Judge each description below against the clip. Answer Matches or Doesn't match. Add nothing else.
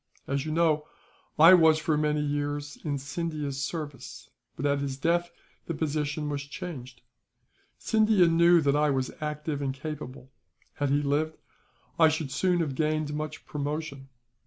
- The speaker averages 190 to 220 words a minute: Doesn't match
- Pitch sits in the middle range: Matches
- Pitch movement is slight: Matches